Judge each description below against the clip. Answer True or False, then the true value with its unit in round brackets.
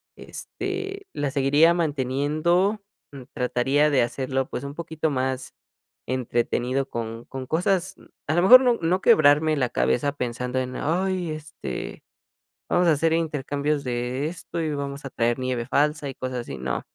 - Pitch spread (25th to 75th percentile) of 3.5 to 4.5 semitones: True (4.1 semitones)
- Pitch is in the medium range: True (145 Hz)